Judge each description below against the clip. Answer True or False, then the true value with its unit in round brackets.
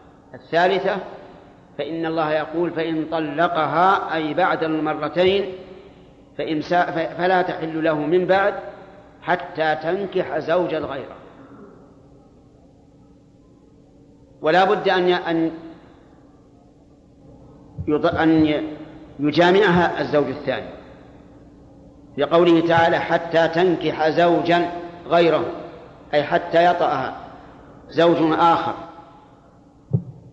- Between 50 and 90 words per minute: True (70 wpm)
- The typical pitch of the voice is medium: True (160 Hz)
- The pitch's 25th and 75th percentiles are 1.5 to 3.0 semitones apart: True (2.7 semitones)